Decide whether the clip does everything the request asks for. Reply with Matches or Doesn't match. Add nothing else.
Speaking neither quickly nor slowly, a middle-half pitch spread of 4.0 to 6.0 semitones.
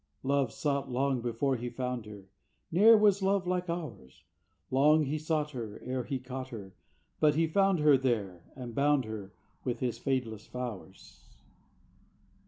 Matches